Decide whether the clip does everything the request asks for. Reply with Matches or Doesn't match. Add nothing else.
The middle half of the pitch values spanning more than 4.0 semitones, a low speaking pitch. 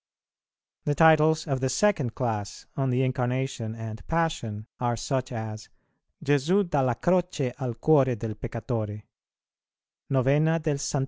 Matches